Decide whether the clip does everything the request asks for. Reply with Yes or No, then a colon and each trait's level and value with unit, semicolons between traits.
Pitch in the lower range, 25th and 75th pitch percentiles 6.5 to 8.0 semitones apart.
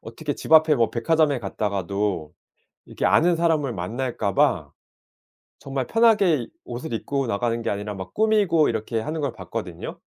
Yes: low, 125 Hz; wide, 6.9 semitones